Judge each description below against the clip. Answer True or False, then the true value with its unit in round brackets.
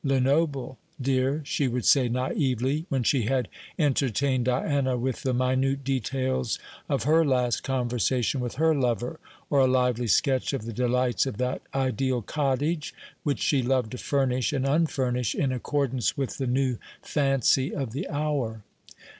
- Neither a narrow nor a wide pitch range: False (1.8 semitones)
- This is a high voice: False (130 Hz)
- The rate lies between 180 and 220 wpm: False (155 wpm)